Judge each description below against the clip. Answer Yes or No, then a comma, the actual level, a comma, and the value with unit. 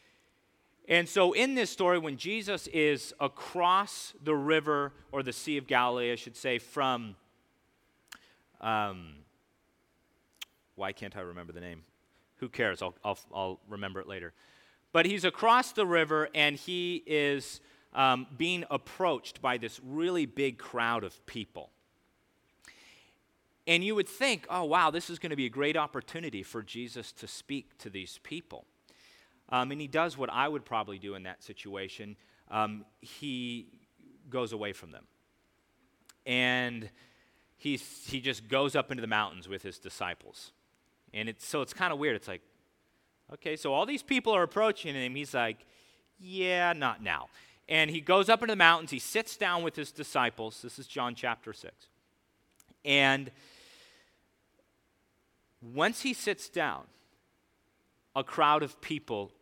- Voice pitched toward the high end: No, low, 135 Hz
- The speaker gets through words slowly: No, average, 155 wpm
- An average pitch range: No, wide, 6.5 semitones